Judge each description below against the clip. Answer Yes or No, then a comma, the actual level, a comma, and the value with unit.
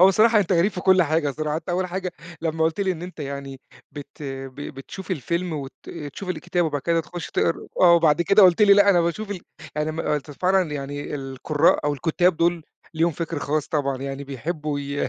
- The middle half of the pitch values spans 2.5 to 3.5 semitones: No, average, 3.9 semitones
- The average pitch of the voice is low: No, medium, 160 Hz